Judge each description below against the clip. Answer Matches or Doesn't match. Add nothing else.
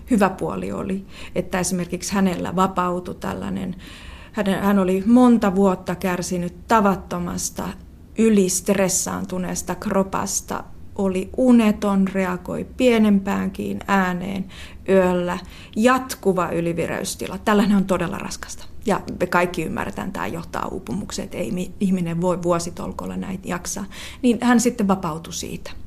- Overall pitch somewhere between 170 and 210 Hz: Matches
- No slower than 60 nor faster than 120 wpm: Matches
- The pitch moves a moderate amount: Doesn't match